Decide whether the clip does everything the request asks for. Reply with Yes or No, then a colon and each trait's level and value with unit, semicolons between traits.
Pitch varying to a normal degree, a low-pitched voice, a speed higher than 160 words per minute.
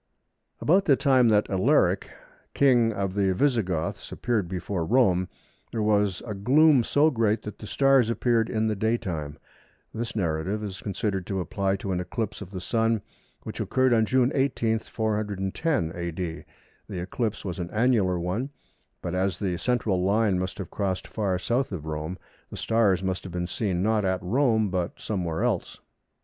Yes: average, 3.9 semitones; low, 105 Hz; average, 170 wpm